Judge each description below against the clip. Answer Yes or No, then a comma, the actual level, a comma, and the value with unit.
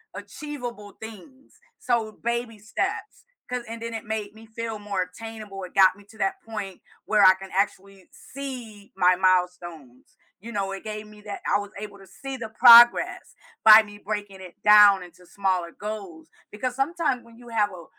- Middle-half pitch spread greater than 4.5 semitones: No, average, 3.0 semitones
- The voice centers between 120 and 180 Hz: No, high, 210 Hz